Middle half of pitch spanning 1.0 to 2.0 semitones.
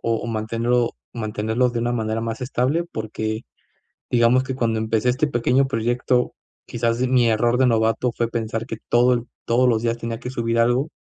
Yes: narrow, 1.6 semitones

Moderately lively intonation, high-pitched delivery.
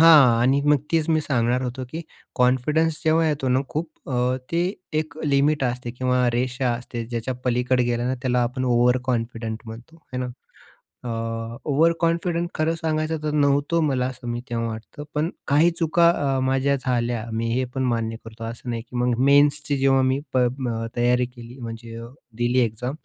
No: average, 3.4 semitones; low, 130 Hz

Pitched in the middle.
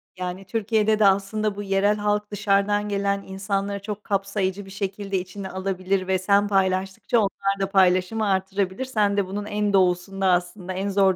No: high, 195 Hz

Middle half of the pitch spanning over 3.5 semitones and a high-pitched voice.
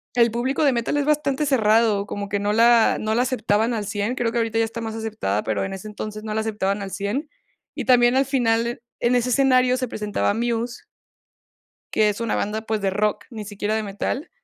No: average, 2.7 semitones; high, 225 Hz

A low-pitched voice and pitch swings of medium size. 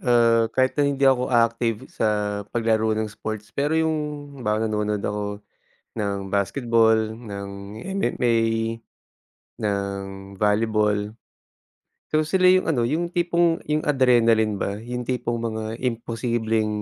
Yes: low, 115 Hz; average, 3.2 semitones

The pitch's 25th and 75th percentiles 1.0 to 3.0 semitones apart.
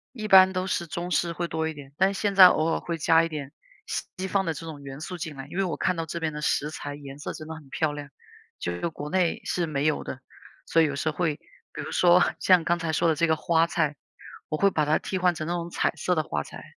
Yes: average, 2.7 semitones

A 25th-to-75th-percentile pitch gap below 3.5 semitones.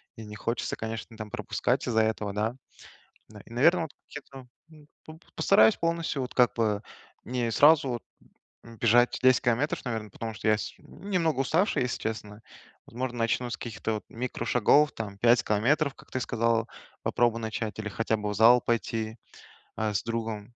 Yes: average, 2.8 semitones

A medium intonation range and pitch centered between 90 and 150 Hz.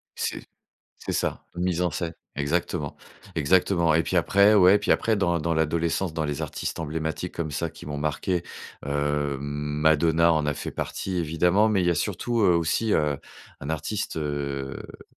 No: average, 3.2 semitones; very low, 80 Hz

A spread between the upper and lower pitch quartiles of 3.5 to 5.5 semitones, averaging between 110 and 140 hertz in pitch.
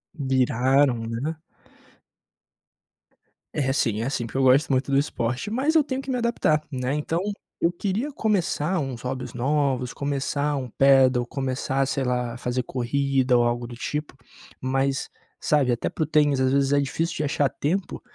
No: average, 2.9 semitones; low, 135 Hz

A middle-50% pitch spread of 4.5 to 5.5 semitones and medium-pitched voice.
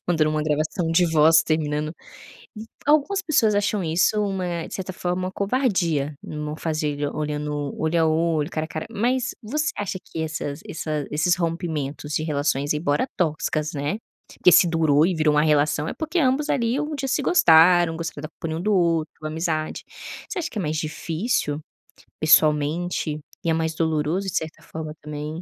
No: average, 3.6 semitones; medium, 160 Hz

